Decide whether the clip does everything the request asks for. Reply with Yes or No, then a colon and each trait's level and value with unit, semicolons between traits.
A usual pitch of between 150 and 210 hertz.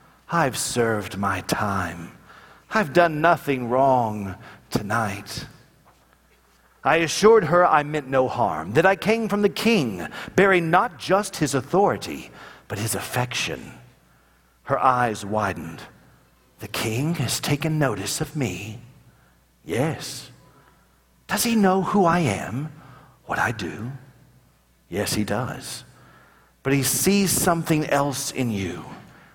No: low, 135 Hz